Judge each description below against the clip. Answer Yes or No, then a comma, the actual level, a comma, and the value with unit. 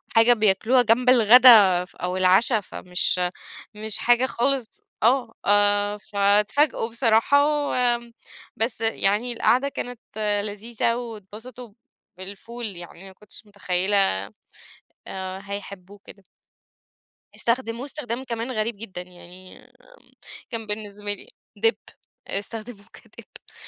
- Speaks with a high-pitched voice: Yes, high, 215 Hz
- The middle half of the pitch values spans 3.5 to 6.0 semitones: No, average, 3.1 semitones